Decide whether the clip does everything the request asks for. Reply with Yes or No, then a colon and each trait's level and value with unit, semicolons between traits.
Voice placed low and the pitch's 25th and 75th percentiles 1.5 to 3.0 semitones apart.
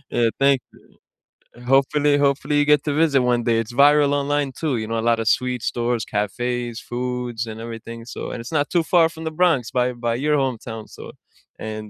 No: low, 125 Hz; average, 3.8 semitones